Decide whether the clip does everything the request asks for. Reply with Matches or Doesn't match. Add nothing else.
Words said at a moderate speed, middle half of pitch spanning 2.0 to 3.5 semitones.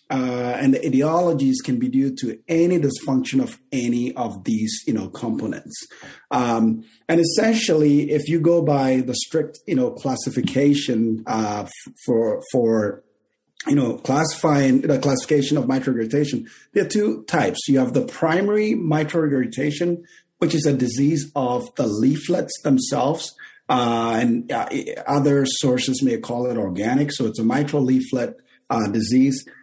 Doesn't match